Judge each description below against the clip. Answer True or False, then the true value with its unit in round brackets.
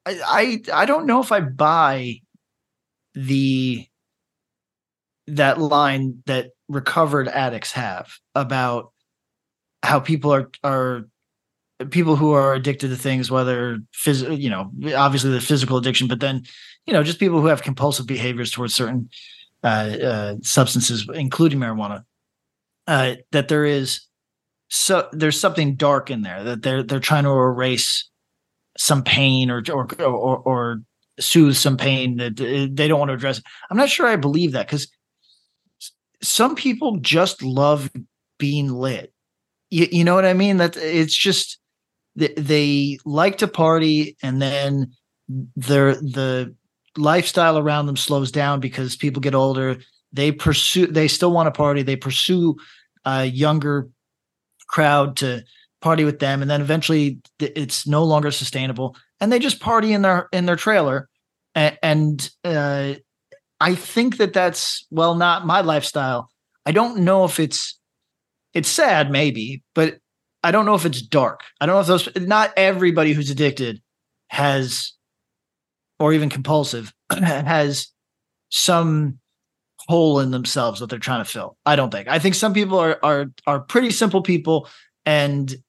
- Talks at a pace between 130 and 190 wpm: True (150 wpm)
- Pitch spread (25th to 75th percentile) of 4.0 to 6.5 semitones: False (3.6 semitones)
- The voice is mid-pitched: True (145 Hz)